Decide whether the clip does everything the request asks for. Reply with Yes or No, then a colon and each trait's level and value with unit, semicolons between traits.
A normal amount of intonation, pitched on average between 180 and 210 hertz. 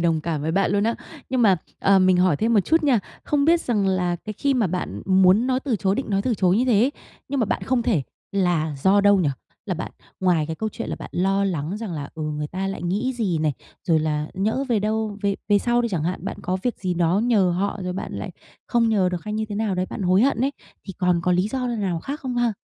Yes: average, 4.3 semitones; high, 195 Hz